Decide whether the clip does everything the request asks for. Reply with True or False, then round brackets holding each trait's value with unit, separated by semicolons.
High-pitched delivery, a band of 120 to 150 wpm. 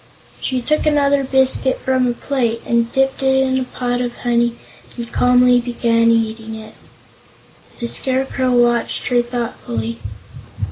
True (245 Hz; 140 wpm)